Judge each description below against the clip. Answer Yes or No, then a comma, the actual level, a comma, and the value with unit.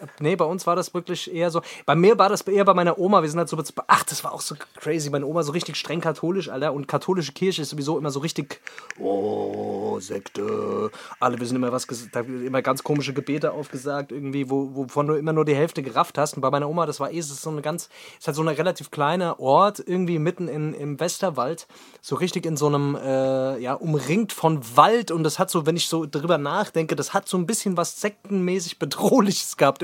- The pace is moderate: No, fast, 235 wpm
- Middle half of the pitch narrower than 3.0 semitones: No, average, 3.5 semitones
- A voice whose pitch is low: No, medium, 160 Hz